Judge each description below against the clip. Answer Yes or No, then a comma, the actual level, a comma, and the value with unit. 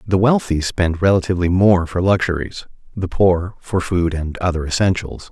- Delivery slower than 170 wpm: Yes, average, 160 wpm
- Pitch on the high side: No, very low, 90 Hz